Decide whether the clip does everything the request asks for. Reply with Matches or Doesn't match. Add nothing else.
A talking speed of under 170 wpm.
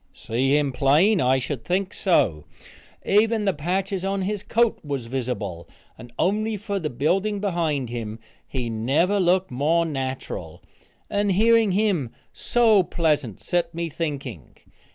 Matches